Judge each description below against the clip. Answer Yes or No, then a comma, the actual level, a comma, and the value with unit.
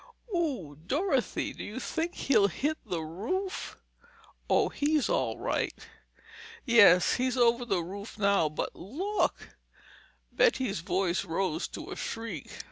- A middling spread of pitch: No, wide, 7.7 semitones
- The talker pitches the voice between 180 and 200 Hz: No, high, 225 Hz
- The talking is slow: Yes, slow, 120 wpm